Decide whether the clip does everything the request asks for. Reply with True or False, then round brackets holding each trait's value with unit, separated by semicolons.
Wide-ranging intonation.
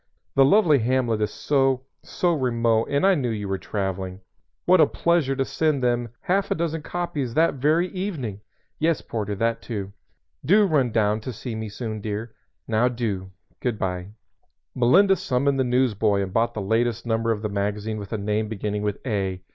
False (5.0 semitones)